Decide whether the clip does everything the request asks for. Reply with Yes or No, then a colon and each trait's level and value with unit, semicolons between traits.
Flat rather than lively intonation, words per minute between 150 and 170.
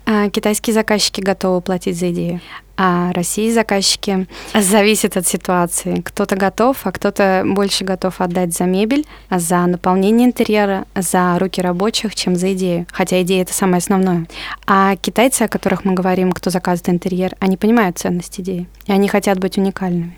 Yes: narrow, 2.0 semitones; fast, 160 wpm